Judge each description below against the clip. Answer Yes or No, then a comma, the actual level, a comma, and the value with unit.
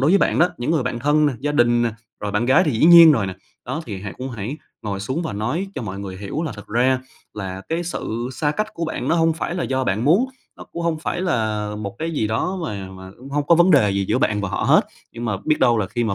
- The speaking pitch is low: Yes, low, 125 Hz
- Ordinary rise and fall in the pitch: No, wide, 7.3 semitones